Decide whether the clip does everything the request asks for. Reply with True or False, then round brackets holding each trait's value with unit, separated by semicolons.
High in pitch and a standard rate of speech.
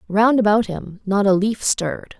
True (205 Hz; 190 wpm)